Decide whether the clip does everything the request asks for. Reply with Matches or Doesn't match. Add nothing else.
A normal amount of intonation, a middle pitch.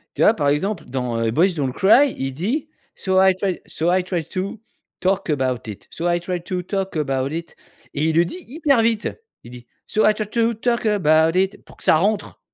Doesn't match